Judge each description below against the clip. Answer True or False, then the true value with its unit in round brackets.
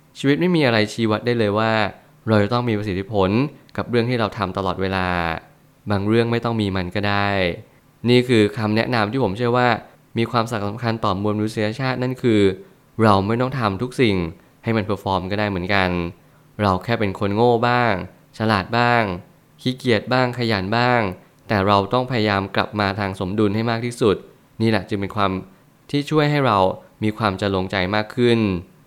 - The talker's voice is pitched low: True (110 Hz)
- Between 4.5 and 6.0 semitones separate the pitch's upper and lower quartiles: False (3.5 semitones)